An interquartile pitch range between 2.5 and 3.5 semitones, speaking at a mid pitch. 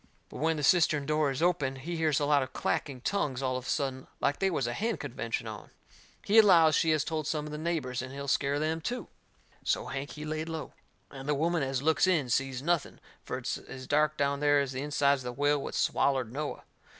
Yes: average, 2.9 semitones; medium, 145 Hz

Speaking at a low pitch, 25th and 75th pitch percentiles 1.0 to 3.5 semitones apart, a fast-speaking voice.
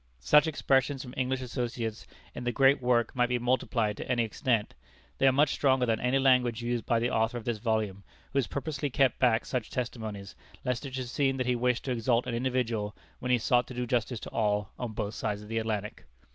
Yes: low, 120 Hz; narrow, 2.4 semitones; fast, 225 wpm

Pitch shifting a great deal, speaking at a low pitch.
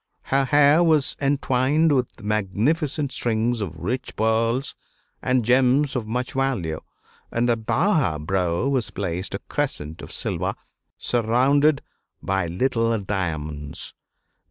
Yes: wide, 5.8 semitones; low, 120 Hz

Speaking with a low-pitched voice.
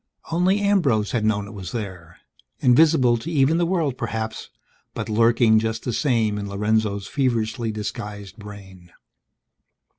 Yes: low, 110 Hz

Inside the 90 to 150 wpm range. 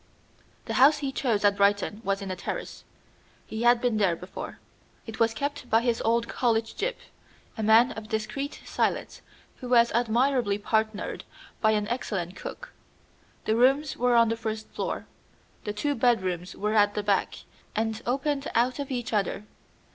No: average, 170 wpm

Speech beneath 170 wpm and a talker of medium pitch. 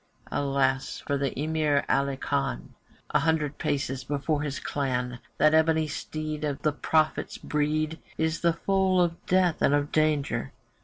Yes: average, 150 wpm; medium, 150 Hz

